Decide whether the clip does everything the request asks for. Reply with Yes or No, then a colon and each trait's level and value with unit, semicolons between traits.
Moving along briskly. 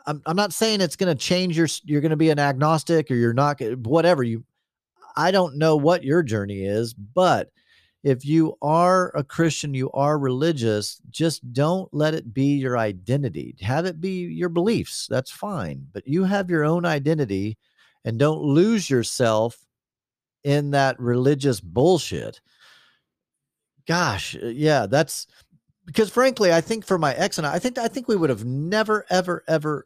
No: average, 175 wpm